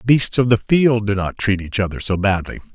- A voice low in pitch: Yes, low, 105 Hz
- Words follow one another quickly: Yes, fast, 260 wpm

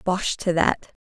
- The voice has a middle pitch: Yes, medium, 180 Hz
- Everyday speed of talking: Yes, average, 175 wpm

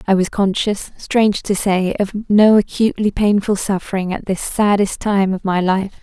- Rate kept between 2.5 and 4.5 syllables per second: No, 4.7 syllables/s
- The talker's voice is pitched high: Yes, high, 200 Hz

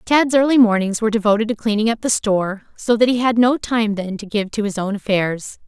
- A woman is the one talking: Yes, female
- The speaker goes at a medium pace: No, fast, 245 wpm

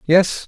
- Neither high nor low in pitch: Yes, medium, 175 Hz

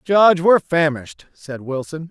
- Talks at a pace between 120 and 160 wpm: Yes, average, 140 wpm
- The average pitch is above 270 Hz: No, medium, 160 Hz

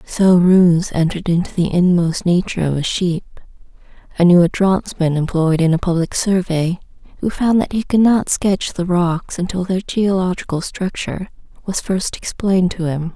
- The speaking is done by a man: No, female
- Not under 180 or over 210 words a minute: No, average, 170 wpm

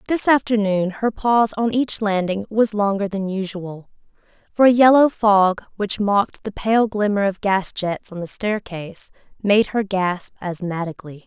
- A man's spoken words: No, female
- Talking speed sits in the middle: Yes, average, 160 wpm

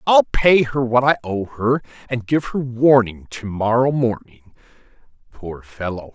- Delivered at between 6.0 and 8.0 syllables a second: No, 4.1 syllables/s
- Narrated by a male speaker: Yes, male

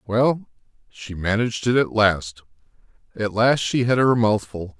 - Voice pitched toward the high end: No, low, 110 Hz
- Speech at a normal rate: Yes, average, 150 wpm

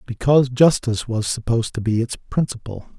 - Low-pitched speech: Yes, low, 120 Hz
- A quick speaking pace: No, average, 160 wpm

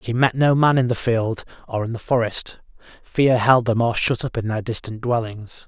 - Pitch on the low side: Yes, low, 120 Hz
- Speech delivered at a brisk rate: Yes, fast, 220 wpm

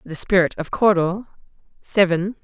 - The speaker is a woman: Yes, female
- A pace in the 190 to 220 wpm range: No, slow, 125 wpm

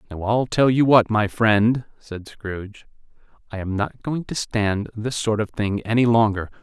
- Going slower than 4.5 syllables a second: Yes, 4.3 syllables/s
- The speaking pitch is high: No, low, 110 Hz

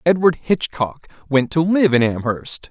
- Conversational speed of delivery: Yes, average, 155 wpm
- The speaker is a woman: No, male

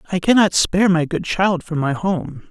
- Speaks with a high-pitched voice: No, medium, 180 Hz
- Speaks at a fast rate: Yes, fast, 215 wpm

